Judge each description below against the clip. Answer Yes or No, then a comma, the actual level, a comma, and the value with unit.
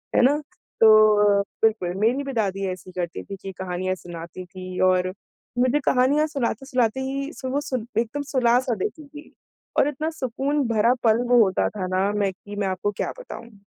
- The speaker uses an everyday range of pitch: No, wide, 5.8 semitones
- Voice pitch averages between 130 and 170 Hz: No, high, 220 Hz